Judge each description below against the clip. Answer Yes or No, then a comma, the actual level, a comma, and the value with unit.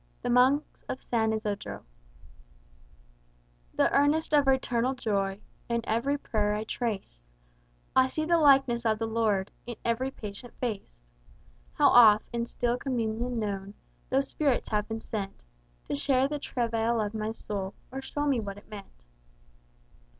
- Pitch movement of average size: Yes, average, 3.8 semitones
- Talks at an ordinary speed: Yes, average, 150 wpm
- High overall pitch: Yes, high, 230 Hz